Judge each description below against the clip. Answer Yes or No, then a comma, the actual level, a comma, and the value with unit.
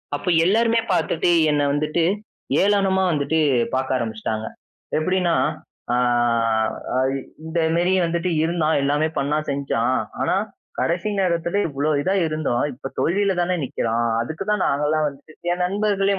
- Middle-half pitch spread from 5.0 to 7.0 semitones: No, average, 4.5 semitones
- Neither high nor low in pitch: Yes, medium, 160 Hz